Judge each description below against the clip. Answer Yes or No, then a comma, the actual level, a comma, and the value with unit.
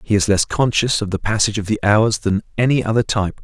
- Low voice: Yes, low, 105 Hz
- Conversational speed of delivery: No, fast, 245 wpm